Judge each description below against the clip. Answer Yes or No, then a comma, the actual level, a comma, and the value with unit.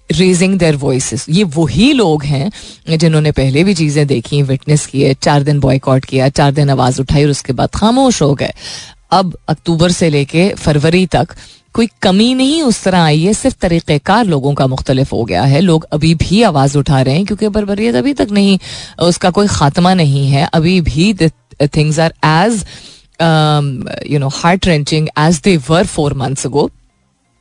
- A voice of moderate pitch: Yes, medium, 155 Hz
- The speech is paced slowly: No, average, 175 wpm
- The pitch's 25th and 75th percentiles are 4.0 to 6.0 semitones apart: Yes, average, 4.6 semitones